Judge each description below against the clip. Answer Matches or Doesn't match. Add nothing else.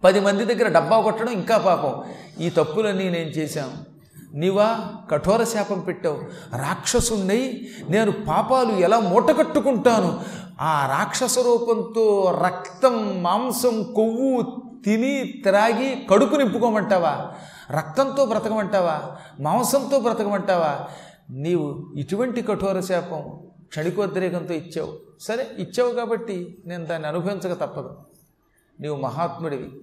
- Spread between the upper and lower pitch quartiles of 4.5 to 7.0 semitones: Matches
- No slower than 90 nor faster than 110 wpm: Matches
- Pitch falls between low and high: Doesn't match